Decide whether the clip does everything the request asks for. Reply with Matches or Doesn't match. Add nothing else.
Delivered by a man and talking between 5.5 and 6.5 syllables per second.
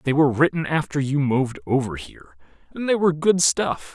Matches